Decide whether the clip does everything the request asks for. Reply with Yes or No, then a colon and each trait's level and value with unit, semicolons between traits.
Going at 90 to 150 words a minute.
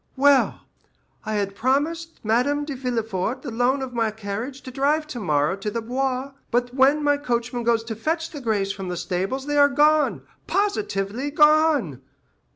No: average, 160 wpm